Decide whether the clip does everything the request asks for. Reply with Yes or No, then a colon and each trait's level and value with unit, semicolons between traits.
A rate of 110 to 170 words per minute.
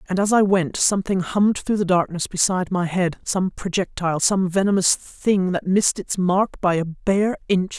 No: average, 195 wpm